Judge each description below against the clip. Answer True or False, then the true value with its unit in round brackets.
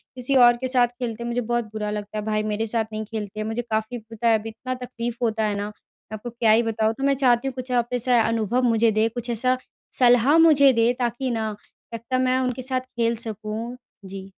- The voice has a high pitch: True (235 Hz)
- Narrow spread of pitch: True (2.2 semitones)